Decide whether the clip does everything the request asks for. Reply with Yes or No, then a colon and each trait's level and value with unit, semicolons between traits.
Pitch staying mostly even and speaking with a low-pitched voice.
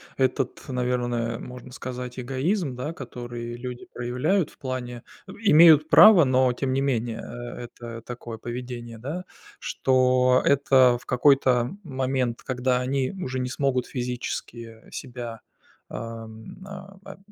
Yes: narrow, 1.9 semitones; low, 125 Hz